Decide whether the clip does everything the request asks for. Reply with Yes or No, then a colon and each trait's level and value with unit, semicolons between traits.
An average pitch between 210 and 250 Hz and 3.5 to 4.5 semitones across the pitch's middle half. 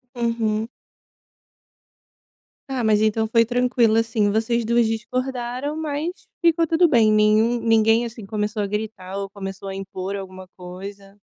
No: high, 220 Hz; average, 2.9 semitones